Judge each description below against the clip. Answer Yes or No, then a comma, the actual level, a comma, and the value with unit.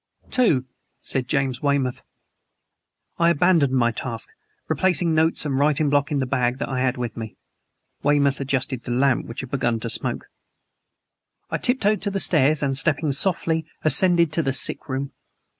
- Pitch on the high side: No, medium, 140 Hz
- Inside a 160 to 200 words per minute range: Yes, average, 165 wpm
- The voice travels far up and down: No, average, 3.7 semitones